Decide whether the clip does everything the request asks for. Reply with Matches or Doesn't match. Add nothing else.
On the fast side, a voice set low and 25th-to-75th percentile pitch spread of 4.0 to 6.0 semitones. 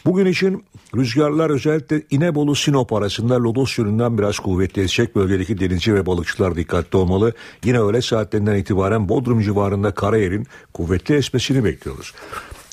Doesn't match